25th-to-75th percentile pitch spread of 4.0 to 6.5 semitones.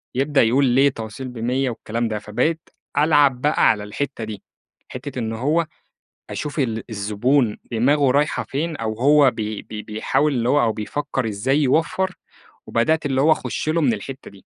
Yes: average, 4.7 semitones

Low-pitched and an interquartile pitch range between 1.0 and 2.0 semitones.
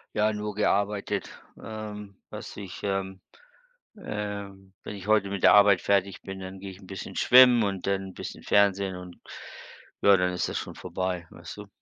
Yes: low, 100 Hz; narrow, 1.5 semitones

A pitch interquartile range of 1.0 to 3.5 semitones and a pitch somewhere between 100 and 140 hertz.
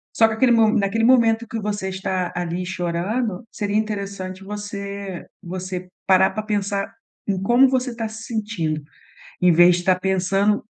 No: average, 2.9 semitones; high, 200 Hz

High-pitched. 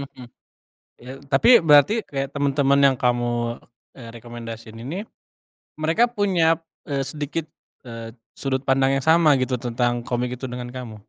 No: low, 135 Hz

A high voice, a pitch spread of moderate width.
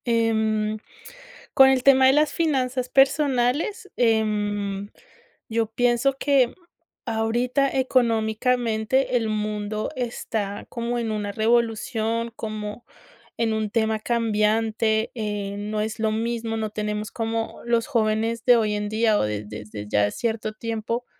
No: high, 225 Hz; narrow, 2.1 semitones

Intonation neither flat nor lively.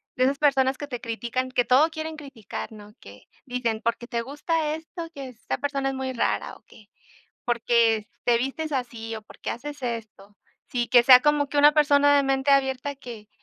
Yes: average, 3.5 semitones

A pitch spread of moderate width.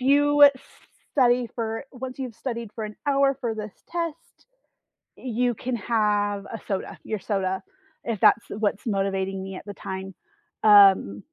Yes: average, 4.1 semitones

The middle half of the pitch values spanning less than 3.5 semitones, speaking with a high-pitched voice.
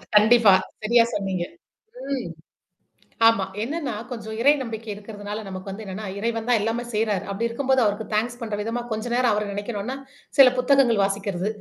Yes: average, 2.8 semitones; high, 220 Hz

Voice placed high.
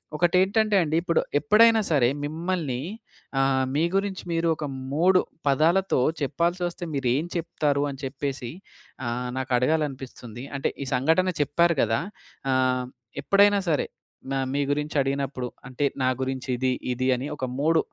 No: medium, 145 Hz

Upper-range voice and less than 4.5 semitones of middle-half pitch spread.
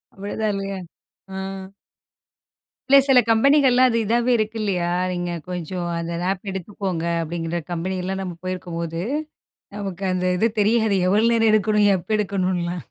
Yes: high, 195 Hz; average, 3.5 semitones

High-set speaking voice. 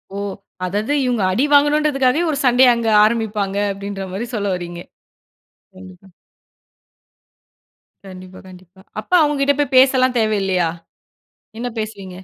Yes: high, 215 Hz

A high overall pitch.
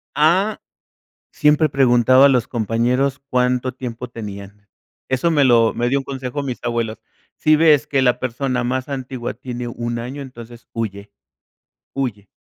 No: low, 125 Hz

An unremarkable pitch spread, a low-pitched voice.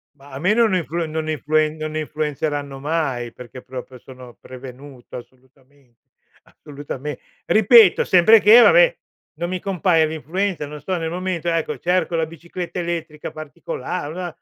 No: average, 3.9 semitones; medium, 155 Hz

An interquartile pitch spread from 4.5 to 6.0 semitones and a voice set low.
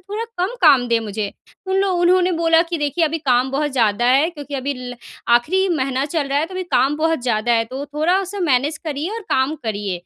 No: average, 5.2 semitones; very high, 290 Hz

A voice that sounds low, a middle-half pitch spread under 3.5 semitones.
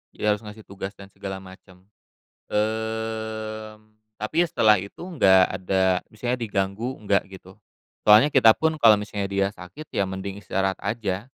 Yes: low, 105 Hz; narrow, 2.4 semitones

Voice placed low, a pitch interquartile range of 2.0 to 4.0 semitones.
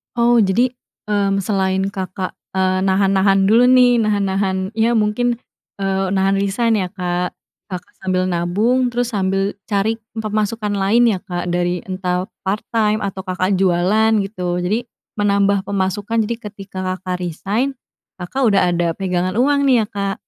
No: high, 195 Hz; average, 2.8 semitones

